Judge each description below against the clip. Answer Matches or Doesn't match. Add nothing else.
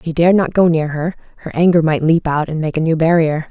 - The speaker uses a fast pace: Matches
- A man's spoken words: Doesn't match